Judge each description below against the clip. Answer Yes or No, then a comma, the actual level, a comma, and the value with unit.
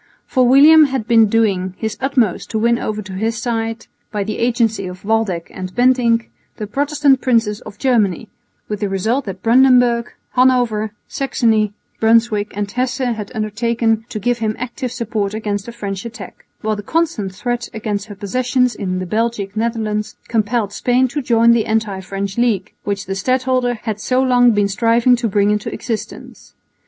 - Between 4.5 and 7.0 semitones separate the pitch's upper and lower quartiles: No, average, 2.9 semitones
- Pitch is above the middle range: Yes, high, 225 Hz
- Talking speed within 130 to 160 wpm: No, average, 170 wpm